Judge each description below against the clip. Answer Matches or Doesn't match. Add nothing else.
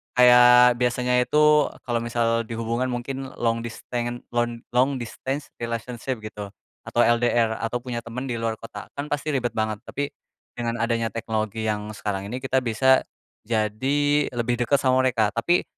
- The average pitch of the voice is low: Matches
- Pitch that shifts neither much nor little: Doesn't match